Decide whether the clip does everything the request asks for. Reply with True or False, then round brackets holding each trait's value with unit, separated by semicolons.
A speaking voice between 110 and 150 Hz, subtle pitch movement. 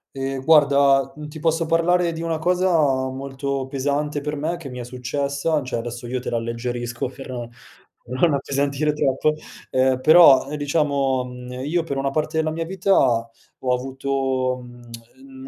False (140 Hz; 3.3 semitones)